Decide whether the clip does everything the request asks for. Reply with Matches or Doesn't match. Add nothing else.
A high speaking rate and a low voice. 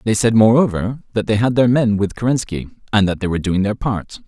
Matches